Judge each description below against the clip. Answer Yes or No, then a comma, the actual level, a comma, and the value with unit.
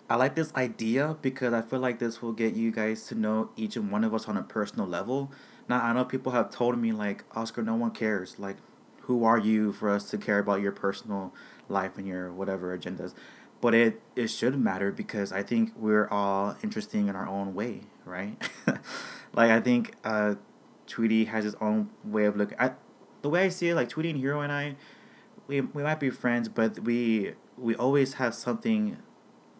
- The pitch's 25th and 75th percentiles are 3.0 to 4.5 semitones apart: Yes, average, 3.8 semitones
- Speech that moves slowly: No, fast, 205 wpm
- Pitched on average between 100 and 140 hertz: Yes, low, 115 Hz